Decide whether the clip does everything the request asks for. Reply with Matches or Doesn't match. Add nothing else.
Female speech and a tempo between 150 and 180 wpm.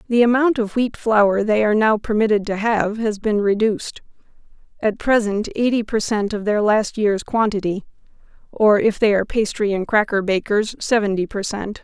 Matches